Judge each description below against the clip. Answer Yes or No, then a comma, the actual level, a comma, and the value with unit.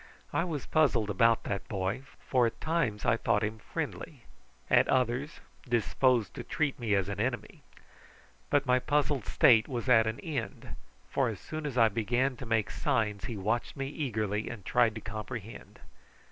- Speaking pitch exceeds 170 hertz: No, low, 115 Hz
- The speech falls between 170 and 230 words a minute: Yes, average, 175 wpm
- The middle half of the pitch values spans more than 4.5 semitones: No, average, 3.5 semitones